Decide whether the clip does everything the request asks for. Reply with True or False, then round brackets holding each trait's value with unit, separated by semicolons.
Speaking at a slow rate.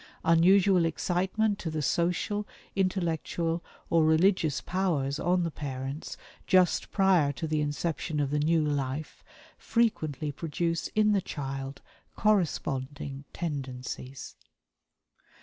True (110 wpm)